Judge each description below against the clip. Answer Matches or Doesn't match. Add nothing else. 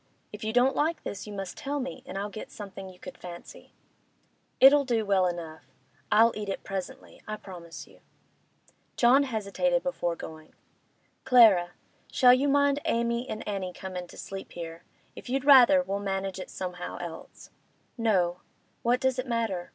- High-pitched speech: Matches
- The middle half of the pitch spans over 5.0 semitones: Matches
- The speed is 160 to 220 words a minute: Matches